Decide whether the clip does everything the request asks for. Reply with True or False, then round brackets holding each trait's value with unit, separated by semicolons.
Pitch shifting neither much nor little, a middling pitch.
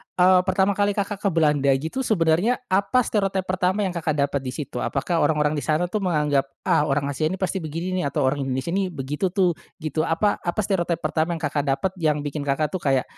True (4.4 semitones; 165 Hz)